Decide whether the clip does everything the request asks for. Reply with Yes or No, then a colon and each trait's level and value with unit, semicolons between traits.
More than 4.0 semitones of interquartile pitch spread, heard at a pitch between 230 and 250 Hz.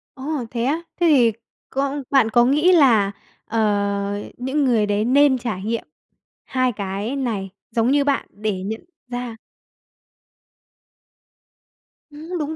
Yes: average, 4.7 semitones; high, 245 Hz